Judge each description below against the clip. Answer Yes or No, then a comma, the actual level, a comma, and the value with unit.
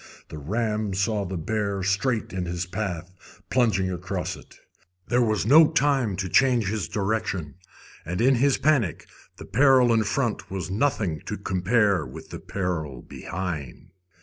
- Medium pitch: No, low, 100 Hz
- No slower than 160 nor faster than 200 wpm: No, average, 150 wpm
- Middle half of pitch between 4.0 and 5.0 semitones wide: Yes, average, 4.5 semitones